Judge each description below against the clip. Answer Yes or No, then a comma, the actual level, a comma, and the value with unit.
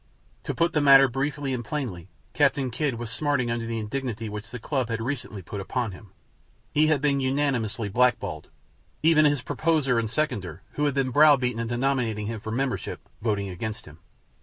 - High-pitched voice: No, low, 125 Hz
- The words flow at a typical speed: Yes, average, 185 wpm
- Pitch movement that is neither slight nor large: Yes, average, 4.3 semitones